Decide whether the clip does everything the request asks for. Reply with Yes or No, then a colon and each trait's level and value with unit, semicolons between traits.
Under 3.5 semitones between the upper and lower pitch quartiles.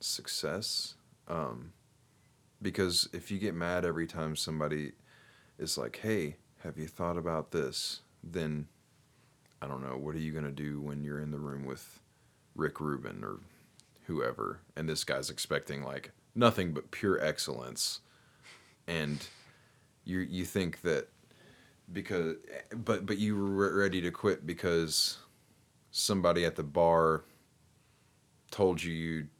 No: average, 4.6 semitones